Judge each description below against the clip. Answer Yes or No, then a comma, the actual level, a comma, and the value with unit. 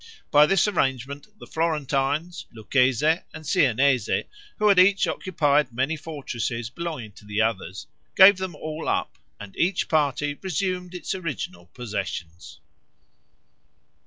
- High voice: No, medium, 145 Hz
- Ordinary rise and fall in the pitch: No, wide, 6.4 semitones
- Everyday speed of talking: No, slow, 125 wpm